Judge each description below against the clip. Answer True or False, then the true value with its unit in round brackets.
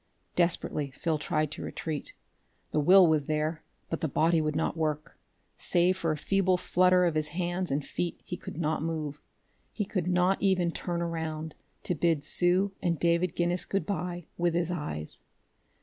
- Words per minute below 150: False (175 wpm)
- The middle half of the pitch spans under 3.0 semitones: True (2.5 semitones)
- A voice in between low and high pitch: True (170 Hz)